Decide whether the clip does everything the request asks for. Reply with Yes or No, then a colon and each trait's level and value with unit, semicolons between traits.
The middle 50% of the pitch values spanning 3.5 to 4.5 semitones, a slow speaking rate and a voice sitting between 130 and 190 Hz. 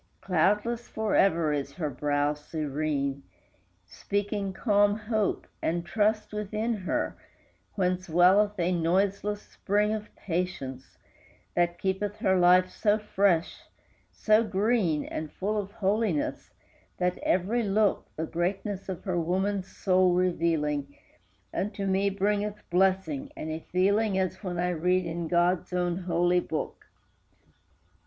No: average, 3.1 semitones; slow, 125 wpm; medium, 185 Hz